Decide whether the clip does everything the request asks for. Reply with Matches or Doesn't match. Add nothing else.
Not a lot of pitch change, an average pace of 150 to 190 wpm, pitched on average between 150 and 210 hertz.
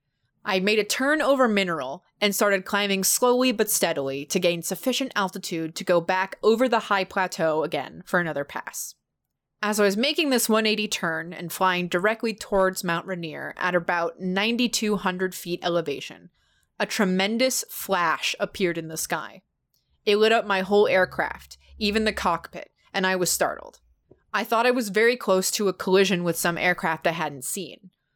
Doesn't match